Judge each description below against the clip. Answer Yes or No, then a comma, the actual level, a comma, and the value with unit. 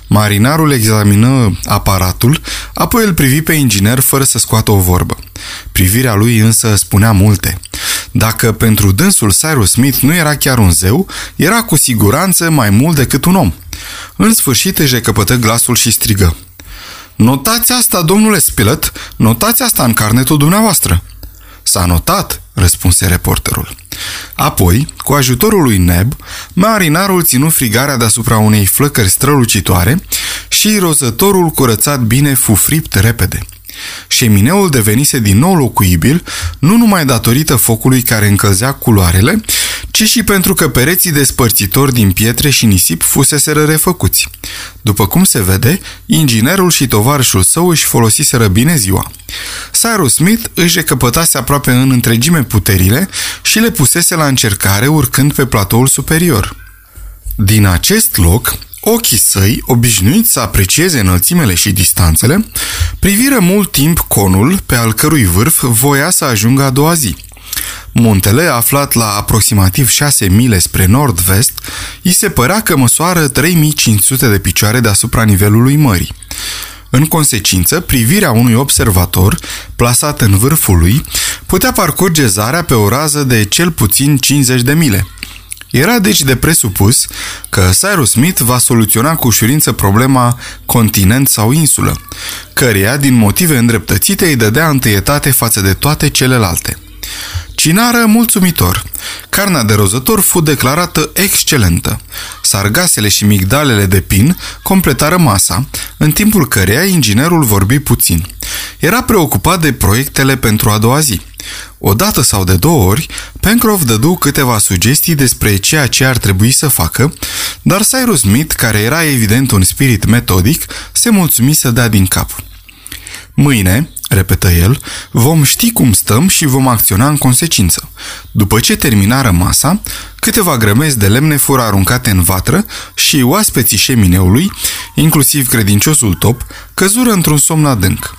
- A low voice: Yes, low, 120 Hz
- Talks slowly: No, average, 135 wpm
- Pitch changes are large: Yes, wide, 6.9 semitones